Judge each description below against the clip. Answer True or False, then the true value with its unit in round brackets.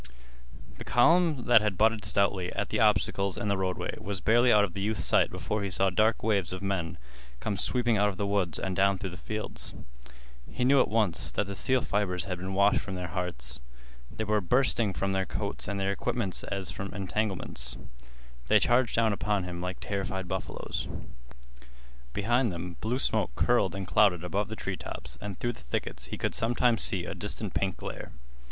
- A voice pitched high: False (100 Hz)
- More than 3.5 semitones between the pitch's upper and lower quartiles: False (2.7 semitones)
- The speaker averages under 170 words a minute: False (195 wpm)